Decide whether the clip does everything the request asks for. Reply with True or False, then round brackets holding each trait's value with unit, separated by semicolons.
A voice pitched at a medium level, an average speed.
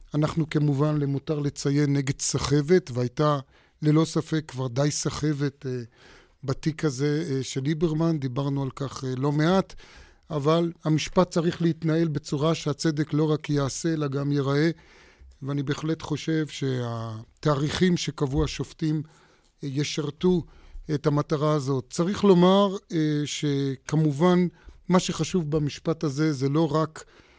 True (150 Hz; 115 wpm)